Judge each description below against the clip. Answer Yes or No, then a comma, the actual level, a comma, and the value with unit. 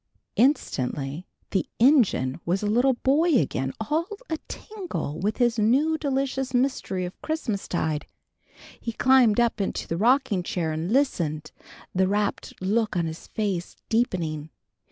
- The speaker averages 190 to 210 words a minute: No, average, 140 wpm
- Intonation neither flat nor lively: No, wide, 7.2 semitones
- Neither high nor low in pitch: No, high, 215 Hz